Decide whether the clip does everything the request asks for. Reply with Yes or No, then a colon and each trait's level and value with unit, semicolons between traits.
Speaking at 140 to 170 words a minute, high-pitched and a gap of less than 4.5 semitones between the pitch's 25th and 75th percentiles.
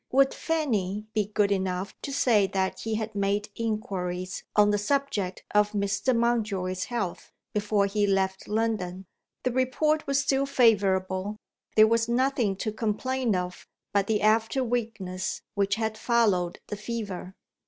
Yes: average, 145 wpm; high, 210 Hz; average, 3.3 semitones